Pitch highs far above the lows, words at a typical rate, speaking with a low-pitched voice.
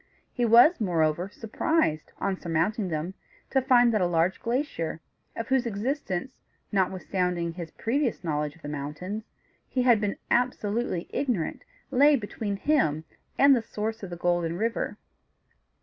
No: wide, 6.0 semitones; average, 145 wpm; high, 205 Hz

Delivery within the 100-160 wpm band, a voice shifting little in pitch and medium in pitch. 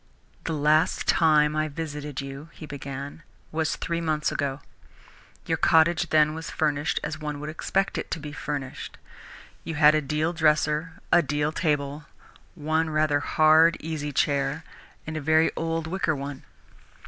Yes: average, 155 wpm; narrow, 1.6 semitones; medium, 155 Hz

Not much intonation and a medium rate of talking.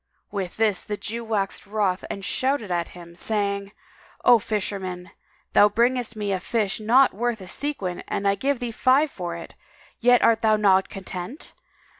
No: average, 3.5 semitones; average, 175 wpm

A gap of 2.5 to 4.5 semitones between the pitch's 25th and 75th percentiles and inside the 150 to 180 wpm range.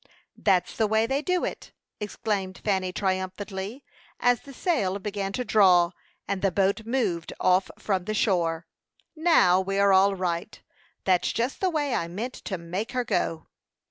Yes: average, 3.7 semitones; average, 165 wpm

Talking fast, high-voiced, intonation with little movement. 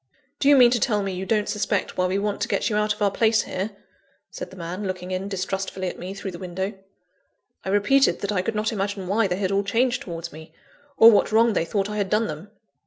Yes: fast, 250 wpm; high, 200 Hz; narrow, 2.3 semitones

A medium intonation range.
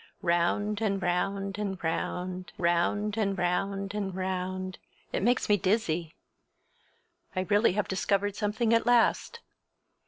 No: narrow, 2.3 semitones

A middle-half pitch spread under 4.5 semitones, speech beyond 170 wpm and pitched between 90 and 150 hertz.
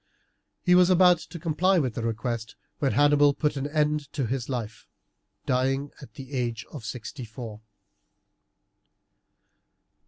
No: average, 4.0 semitones; slow, 135 wpm; medium, 140 Hz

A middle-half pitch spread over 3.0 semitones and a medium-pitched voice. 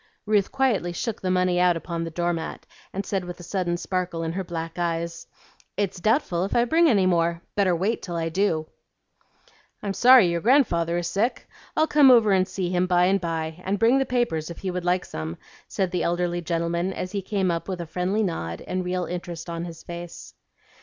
No: narrow, 2.6 semitones; medium, 180 Hz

